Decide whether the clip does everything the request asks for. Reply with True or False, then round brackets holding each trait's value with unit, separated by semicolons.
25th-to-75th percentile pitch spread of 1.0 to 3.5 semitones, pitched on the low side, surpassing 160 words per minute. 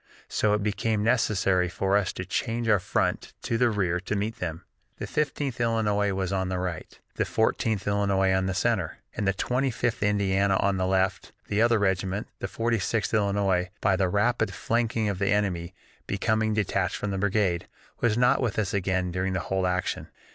True (2.7 semitones; 100 Hz; 190 wpm)